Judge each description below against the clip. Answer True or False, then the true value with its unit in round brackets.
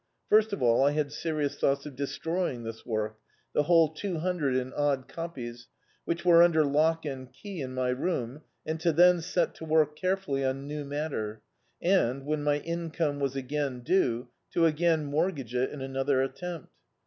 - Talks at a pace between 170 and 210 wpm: True (185 wpm)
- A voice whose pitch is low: False (145 Hz)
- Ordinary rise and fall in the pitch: True (4.0 semitones)